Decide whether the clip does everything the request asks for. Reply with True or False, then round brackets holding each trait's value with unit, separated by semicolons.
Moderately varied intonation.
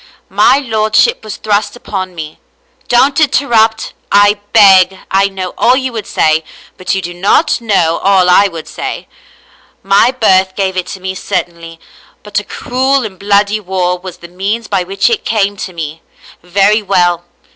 True (3.1 semitones)